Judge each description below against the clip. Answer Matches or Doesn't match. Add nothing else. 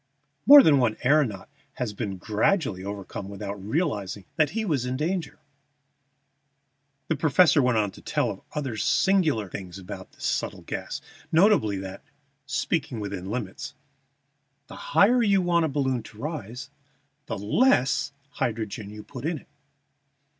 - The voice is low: Matches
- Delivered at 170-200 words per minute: Doesn't match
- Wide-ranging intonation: Matches